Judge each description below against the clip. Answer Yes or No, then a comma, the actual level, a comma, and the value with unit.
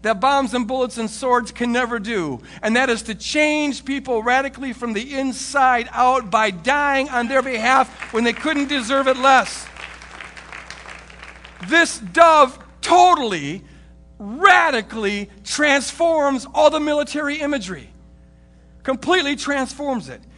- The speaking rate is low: Yes, slow, 125 wpm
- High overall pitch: Yes, very high, 255 Hz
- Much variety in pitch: No, average, 4.0 semitones